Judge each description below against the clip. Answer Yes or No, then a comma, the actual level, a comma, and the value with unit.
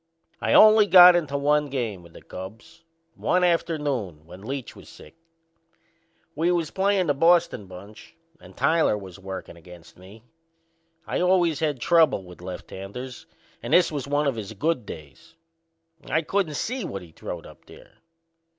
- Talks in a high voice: No, medium, 140 Hz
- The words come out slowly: No, average, 160 wpm